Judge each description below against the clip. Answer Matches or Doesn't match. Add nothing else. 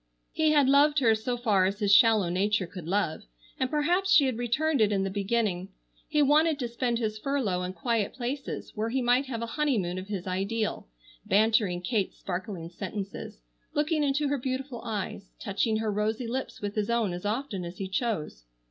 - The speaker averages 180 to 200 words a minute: Matches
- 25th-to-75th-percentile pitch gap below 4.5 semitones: Doesn't match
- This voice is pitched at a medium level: Doesn't match